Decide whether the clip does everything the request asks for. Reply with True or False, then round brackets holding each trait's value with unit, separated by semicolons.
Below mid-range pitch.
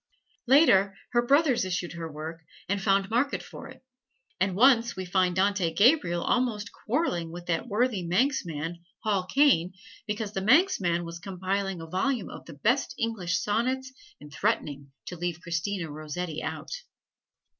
False (195 Hz)